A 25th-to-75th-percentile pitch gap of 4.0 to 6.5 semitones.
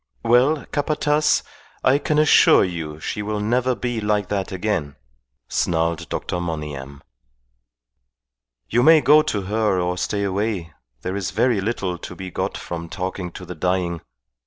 Yes: average, 5.1 semitones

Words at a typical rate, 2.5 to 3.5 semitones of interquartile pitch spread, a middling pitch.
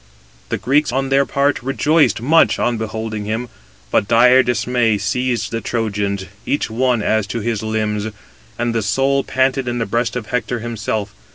No: average, 170 wpm; average, 2.8 semitones; low, 115 Hz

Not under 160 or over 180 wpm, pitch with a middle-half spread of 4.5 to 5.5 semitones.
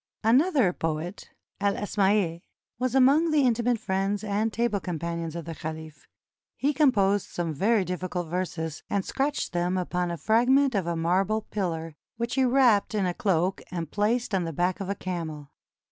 Yes: average, 170 wpm; average, 5.0 semitones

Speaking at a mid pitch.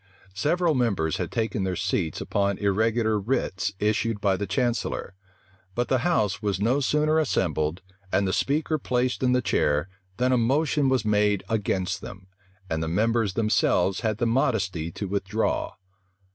No: low, 105 Hz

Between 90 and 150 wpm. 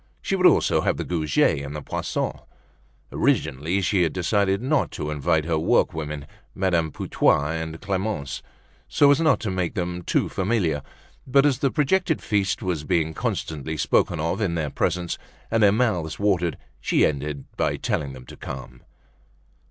No: average, 165 wpm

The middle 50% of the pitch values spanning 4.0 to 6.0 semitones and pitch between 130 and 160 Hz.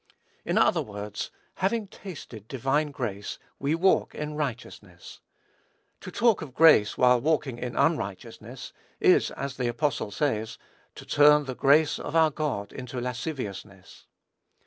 Yes: average, 5.2 semitones; low, 135 Hz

